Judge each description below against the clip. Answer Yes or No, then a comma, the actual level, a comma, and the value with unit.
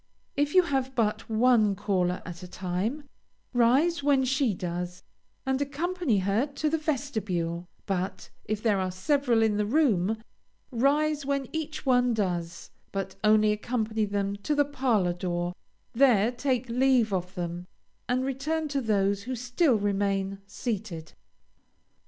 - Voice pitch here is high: Yes, high, 225 Hz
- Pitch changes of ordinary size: No, wide, 5.7 semitones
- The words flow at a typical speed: Yes, average, 145 wpm